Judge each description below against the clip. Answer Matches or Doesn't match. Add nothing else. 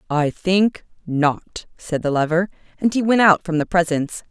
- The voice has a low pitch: Doesn't match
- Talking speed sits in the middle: Matches